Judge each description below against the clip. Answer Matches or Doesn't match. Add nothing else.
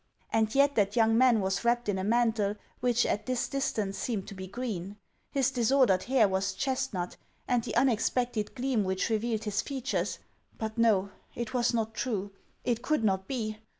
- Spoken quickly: Doesn't match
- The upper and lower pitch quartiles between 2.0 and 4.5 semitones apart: Matches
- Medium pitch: Doesn't match